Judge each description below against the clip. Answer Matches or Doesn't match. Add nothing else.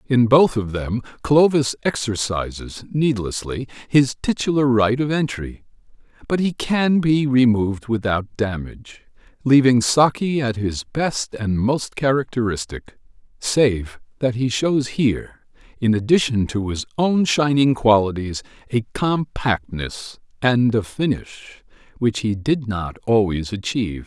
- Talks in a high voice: Doesn't match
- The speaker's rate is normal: Doesn't match